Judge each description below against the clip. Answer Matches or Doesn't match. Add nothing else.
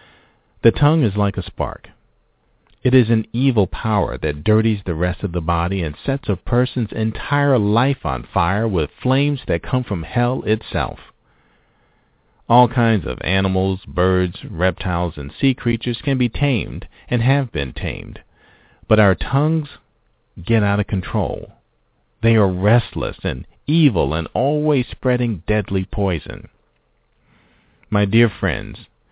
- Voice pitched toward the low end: Matches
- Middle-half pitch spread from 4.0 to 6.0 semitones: Matches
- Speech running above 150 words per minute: Doesn't match